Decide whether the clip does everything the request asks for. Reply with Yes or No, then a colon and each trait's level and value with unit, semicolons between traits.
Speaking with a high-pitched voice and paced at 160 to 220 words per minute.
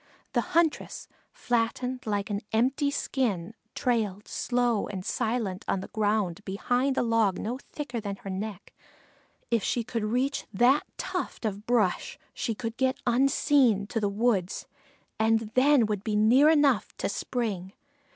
No: high, 225 Hz; average, 150 wpm